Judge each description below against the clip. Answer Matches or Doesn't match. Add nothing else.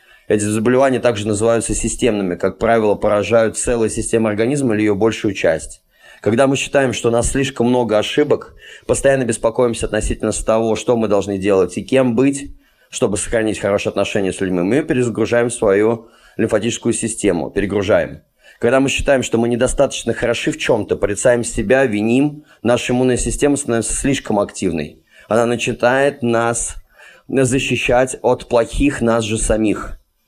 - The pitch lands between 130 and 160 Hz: Doesn't match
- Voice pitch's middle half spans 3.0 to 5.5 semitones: Doesn't match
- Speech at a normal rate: Matches